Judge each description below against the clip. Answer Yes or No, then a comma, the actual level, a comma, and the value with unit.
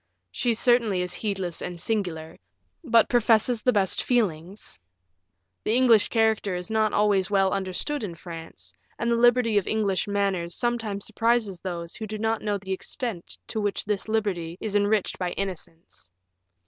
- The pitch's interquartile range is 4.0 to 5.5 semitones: No, average, 3.5 semitones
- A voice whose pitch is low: No, high, 205 Hz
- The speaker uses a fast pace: No, average, 160 wpm